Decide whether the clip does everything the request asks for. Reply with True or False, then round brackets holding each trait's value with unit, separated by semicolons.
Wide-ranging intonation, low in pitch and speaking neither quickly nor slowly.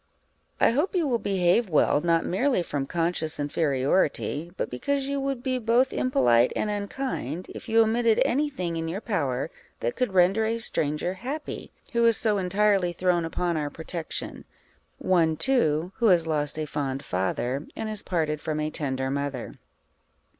False (7.0 semitones; 175 Hz; 170 wpm)